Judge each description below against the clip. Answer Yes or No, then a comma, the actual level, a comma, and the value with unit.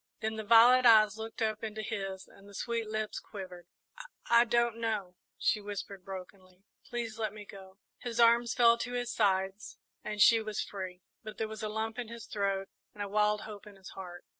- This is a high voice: Yes, high, 215 Hz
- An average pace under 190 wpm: No, fast, 205 wpm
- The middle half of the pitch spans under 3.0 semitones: Yes, narrow, 2.6 semitones